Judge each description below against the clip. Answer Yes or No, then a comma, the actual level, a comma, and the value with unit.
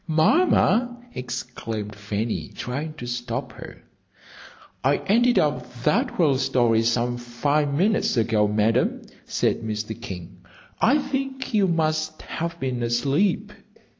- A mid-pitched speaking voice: No, low, 130 Hz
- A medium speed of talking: No, slow, 115 wpm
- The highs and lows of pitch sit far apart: Yes, wide, 6.2 semitones